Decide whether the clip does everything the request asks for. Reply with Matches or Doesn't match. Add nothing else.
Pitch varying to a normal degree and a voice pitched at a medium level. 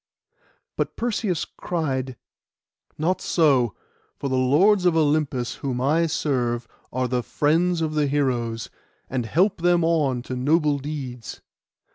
Matches